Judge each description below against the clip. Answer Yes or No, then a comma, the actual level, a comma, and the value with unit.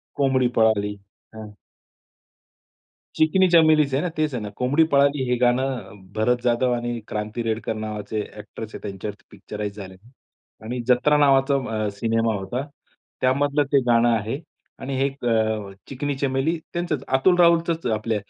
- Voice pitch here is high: No, low, 125 Hz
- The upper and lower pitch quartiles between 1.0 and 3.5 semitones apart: No, average, 4.4 semitones